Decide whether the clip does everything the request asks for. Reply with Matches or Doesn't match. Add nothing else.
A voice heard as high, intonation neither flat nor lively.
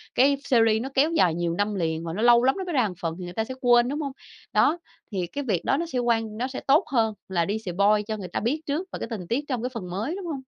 Doesn't match